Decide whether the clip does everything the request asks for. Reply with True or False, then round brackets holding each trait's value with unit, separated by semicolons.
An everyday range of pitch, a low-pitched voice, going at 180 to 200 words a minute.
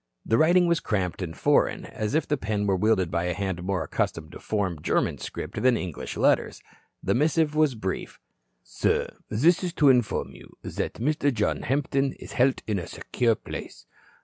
False (7.4 semitones; 110 Hz; 185 wpm)